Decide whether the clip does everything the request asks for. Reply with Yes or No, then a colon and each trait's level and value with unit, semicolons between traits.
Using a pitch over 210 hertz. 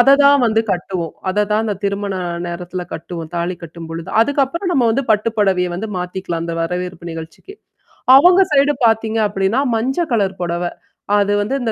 No: high, 200 Hz